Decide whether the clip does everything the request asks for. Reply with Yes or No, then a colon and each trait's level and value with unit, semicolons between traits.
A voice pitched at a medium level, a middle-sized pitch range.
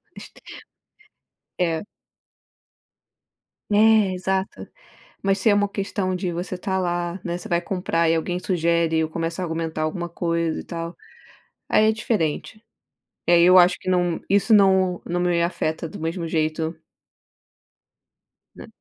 No: medium, 175 Hz; narrow, 2.2 semitones